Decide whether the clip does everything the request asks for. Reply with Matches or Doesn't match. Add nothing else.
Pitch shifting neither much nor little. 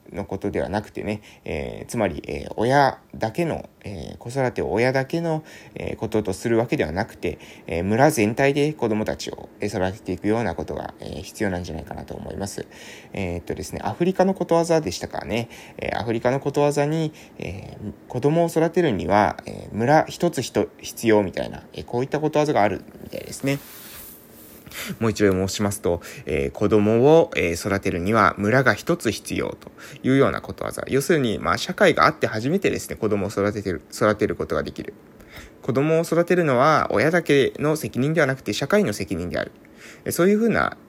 Doesn't match